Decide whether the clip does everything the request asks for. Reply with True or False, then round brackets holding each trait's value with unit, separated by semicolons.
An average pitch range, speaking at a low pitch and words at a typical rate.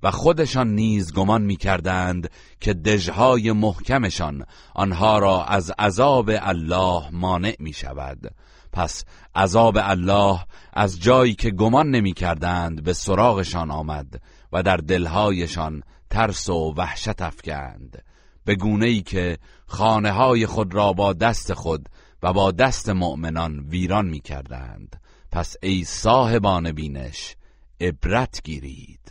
True (4.5 semitones; 95 Hz; 125 wpm)